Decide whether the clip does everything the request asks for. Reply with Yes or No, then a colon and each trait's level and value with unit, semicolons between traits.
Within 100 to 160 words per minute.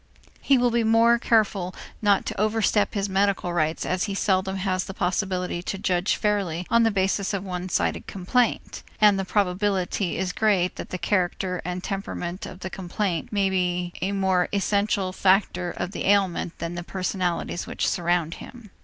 No: average, 180 wpm